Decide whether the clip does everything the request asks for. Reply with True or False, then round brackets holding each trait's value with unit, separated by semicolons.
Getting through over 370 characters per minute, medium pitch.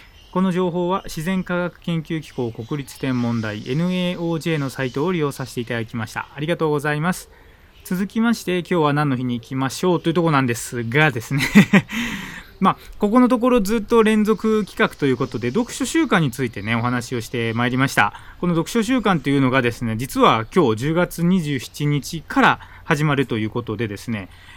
True (380 characters per minute; 150 Hz)